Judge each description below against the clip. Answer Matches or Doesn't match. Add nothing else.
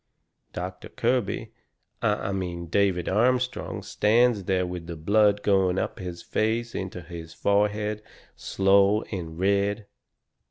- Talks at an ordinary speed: Doesn't match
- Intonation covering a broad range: Doesn't match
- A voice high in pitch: Doesn't match